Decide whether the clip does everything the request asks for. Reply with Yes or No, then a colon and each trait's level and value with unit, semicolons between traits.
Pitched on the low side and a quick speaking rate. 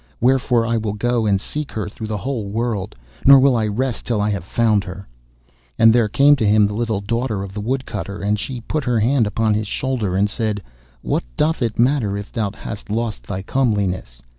Yes: low, 110 Hz; fast, 215 wpm